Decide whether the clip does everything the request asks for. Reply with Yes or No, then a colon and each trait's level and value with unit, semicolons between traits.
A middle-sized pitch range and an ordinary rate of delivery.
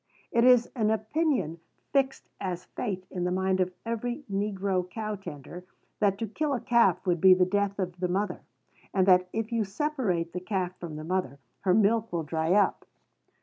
Yes: average, 3.6 semitones; average, 190 wpm